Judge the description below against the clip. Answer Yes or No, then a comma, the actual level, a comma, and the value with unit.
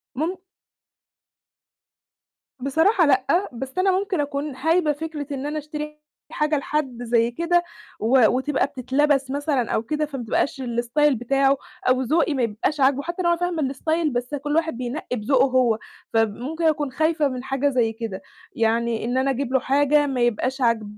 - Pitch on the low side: No, very high, 275 Hz